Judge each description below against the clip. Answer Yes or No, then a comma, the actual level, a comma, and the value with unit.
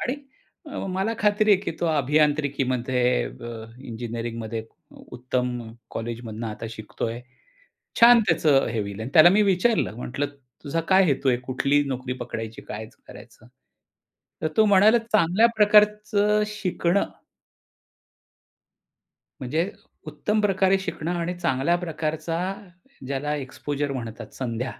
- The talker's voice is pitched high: No, medium, 145 Hz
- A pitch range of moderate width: No, wide, 7.7 semitones